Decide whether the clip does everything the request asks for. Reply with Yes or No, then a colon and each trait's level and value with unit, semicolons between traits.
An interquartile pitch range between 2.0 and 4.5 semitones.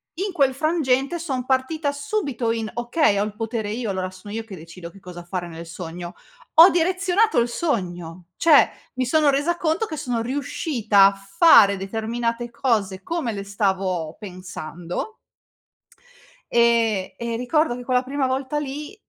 No: wide, 6.7 semitones